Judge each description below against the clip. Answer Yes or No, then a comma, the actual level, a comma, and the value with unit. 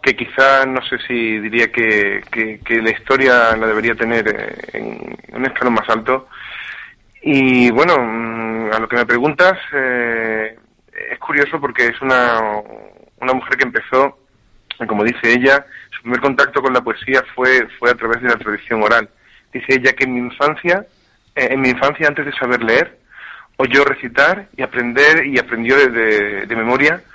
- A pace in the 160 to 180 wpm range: Yes, average, 170 wpm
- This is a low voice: Yes, low, 120 Hz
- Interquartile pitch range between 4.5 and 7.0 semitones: No, average, 2.8 semitones